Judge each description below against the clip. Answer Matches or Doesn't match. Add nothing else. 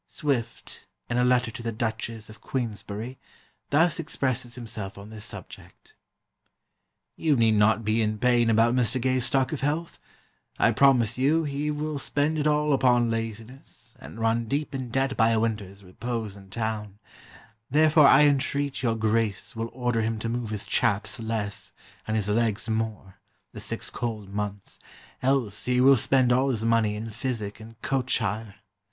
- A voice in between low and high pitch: Doesn't match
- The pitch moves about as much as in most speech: Matches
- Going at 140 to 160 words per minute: Doesn't match